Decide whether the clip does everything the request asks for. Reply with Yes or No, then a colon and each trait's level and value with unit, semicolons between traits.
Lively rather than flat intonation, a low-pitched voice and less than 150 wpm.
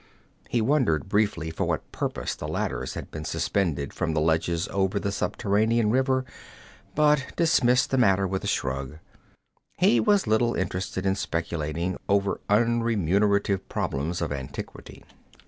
Yes: wide, 5.9 semitones; low, 100 Hz; average, 140 wpm